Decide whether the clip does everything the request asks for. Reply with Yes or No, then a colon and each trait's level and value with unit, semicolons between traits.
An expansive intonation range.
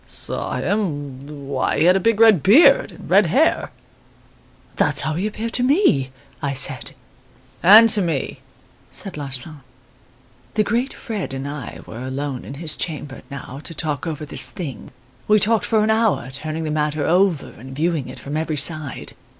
Yes: wide, 6.8 semitones